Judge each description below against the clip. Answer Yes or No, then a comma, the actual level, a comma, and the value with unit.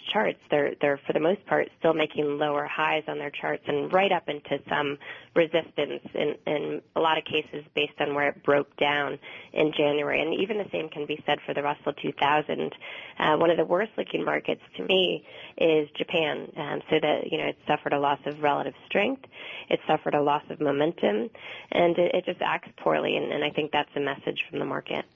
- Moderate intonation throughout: No, narrow, 1.5 semitones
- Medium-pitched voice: Yes, medium, 150 Hz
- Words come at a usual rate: No, fast, 215 wpm